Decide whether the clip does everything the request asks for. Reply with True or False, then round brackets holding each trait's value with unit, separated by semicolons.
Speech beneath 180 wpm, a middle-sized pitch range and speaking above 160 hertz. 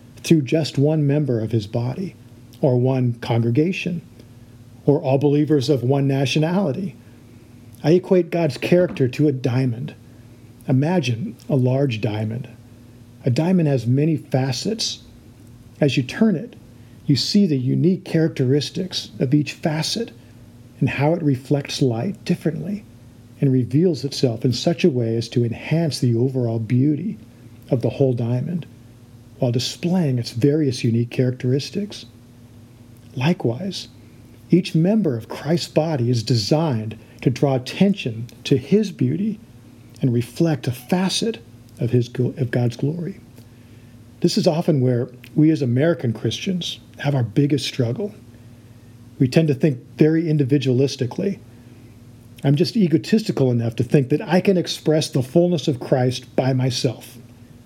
False (135 wpm; 4.6 semitones; 130 Hz)